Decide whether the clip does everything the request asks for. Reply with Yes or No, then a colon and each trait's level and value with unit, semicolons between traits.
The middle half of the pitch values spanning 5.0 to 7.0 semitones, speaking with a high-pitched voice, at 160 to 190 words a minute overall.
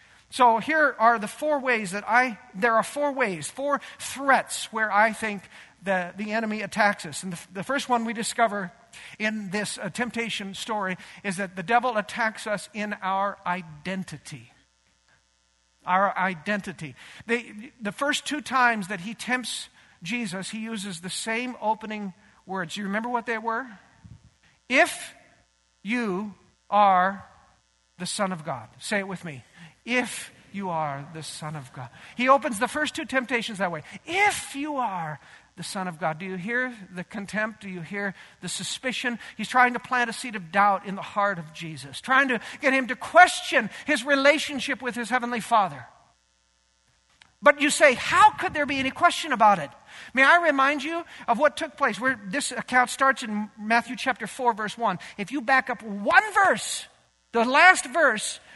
Yes: average, 5.3 semitones; high, 215 Hz; average, 175 wpm